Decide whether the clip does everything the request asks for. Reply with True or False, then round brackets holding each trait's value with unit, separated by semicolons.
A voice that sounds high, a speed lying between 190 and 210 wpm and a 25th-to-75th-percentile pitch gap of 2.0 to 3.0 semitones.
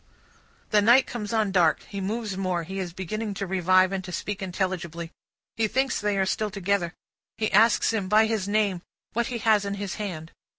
True (200 Hz; 200 wpm; 2.5 semitones)